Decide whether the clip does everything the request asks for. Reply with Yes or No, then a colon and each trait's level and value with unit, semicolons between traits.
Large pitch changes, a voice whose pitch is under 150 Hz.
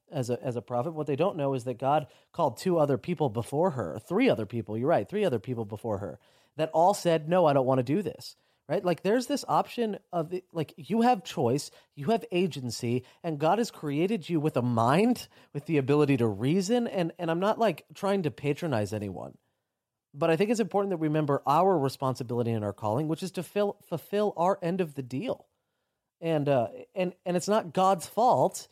No: wide, 6.1 semitones; medium, 160 Hz